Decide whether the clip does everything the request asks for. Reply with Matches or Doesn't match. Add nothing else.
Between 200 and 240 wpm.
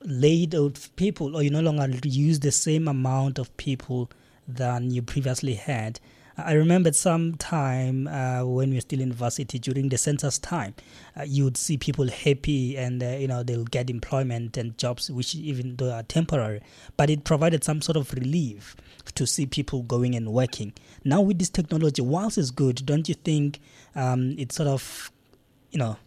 Doesn't match